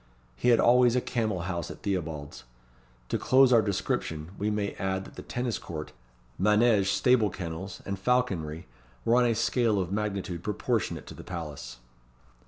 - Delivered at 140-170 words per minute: Yes, average, 165 wpm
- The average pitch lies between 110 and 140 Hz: No, low, 100 Hz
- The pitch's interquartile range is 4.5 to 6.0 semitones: Yes, average, 5.1 semitones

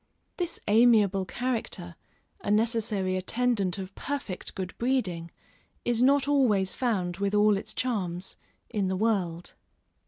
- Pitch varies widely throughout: No, average, 4.5 semitones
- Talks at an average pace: No, slow, 125 wpm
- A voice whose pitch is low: No, high, 205 Hz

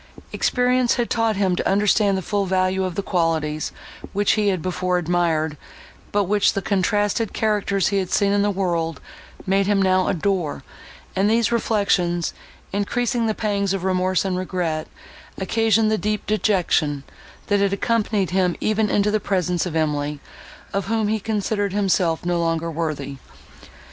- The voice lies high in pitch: Yes, high, 195 Hz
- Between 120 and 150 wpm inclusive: No, average, 160 wpm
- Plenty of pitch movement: No, average, 2.9 semitones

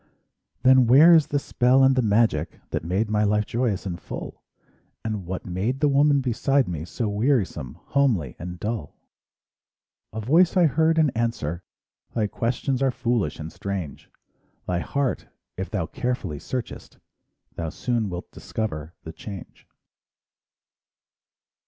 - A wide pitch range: Yes, wide, 6.6 semitones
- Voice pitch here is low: Yes, low, 110 Hz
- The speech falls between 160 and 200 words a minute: No, average, 150 wpm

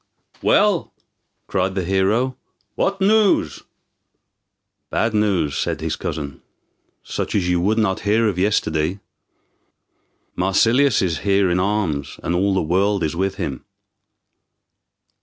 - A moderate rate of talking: No, slow, 120 wpm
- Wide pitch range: No, average, 3.3 semitones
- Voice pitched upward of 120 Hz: No, very low, 95 Hz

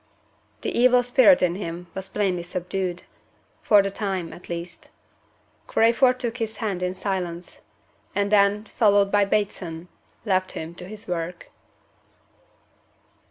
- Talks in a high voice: Yes, high, 195 Hz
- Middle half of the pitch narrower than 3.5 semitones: Yes, average, 3.1 semitones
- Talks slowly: Yes, slow, 130 wpm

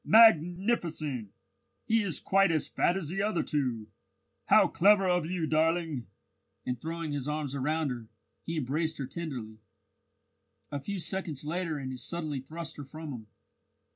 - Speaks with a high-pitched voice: No, medium, 155 Hz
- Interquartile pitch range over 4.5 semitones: No, average, 4.2 semitones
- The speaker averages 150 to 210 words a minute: Yes, average, 155 wpm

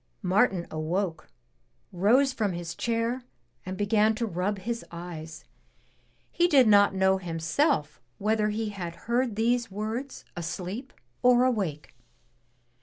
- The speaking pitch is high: Yes, high, 205 Hz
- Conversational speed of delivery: No, slow, 120 wpm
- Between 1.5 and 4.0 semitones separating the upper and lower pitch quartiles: No, average, 5.0 semitones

